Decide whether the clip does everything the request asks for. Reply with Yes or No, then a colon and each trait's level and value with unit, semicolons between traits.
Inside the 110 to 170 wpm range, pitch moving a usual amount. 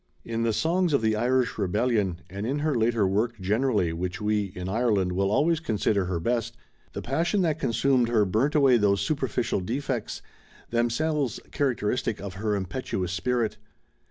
Yes: average, 160 wpm; average, 4.5 semitones